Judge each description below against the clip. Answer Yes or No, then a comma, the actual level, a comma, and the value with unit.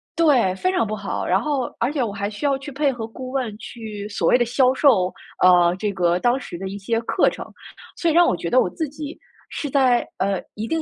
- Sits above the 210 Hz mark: Yes, high, 240 Hz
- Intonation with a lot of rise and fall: Yes, wide, 5.7 semitones